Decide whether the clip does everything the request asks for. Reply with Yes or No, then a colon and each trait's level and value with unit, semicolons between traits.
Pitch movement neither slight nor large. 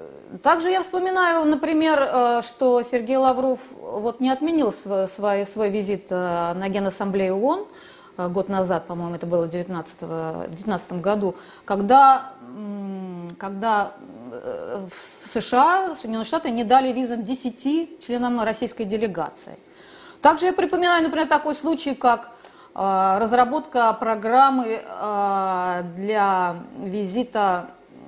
No: wide, 6.2 semitones